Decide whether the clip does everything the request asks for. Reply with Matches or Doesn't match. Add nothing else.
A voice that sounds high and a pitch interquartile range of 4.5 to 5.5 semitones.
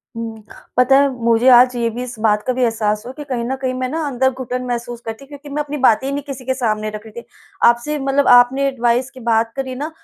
Doesn't match